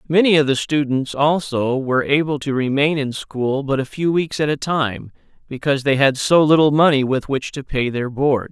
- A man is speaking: Yes, male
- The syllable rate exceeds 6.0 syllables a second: No, 5.0 syllables/s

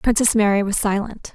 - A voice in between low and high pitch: No, high, 210 Hz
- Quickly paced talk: No, average, 180 wpm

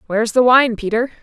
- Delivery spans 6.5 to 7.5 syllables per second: Yes, 7.3 syllables/s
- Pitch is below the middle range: No, high, 230 Hz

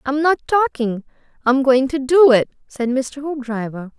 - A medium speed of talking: Yes, average, 165 wpm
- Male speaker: No, female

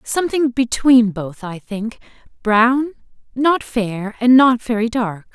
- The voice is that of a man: No, female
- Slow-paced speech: Yes, slow, 125 wpm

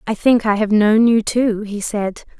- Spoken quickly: Yes, fast, 225 wpm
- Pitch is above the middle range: Yes, high, 215 Hz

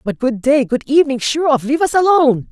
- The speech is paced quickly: Yes, fast, 240 wpm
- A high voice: Yes, very high, 275 Hz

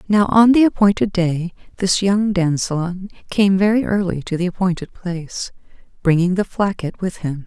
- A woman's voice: Yes, female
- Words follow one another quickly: No, average, 160 wpm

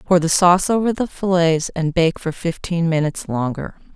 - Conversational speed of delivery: Yes, average, 180 wpm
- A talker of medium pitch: Yes, medium, 170 Hz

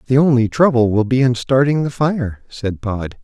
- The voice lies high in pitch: No, low, 125 Hz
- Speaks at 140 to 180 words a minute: No, fast, 205 wpm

